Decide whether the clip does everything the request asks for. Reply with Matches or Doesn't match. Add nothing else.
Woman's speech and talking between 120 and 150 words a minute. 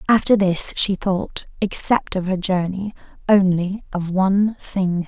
Matches